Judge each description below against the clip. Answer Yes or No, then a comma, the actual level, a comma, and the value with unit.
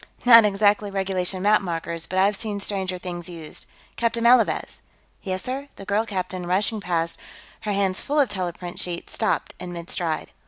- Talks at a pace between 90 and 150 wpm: No, average, 170 wpm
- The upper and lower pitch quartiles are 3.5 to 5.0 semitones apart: No, average, 3.0 semitones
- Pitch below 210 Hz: Yes, high, 190 Hz